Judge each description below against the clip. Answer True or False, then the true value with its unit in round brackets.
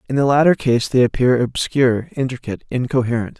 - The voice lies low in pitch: True (125 Hz)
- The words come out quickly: False (160 wpm)